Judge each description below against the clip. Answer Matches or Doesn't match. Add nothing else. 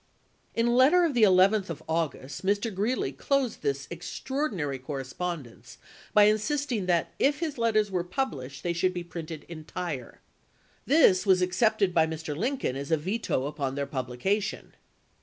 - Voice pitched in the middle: Matches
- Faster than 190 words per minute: Doesn't match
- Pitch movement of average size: Doesn't match